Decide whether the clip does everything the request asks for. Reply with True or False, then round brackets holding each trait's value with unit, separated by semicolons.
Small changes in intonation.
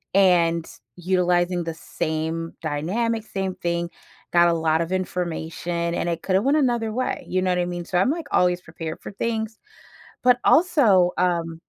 False (3.1 semitones)